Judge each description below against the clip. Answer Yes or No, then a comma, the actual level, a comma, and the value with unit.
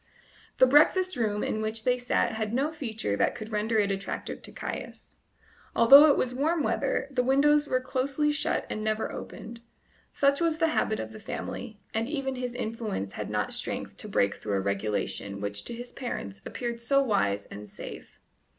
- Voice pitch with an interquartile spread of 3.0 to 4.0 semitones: No, average, 4.7 semitones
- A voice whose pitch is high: Yes, high, 235 Hz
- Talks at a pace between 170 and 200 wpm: Yes, average, 185 wpm